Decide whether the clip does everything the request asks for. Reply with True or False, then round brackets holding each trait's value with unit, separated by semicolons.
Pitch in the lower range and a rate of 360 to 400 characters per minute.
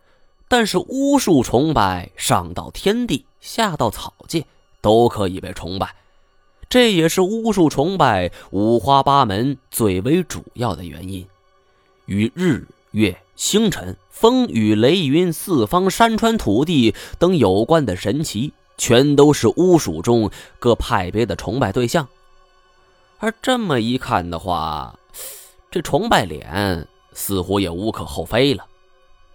False (120 Hz; 190 characters per minute)